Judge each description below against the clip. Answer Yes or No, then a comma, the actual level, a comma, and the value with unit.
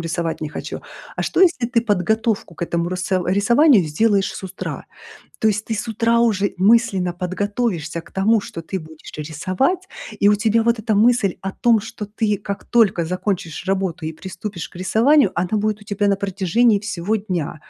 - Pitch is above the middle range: Yes, high, 200 Hz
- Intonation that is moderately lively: Yes, average, 3.7 semitones